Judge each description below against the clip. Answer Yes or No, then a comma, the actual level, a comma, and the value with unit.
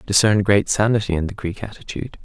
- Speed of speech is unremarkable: No, fast, 215 wpm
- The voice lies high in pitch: No, low, 100 Hz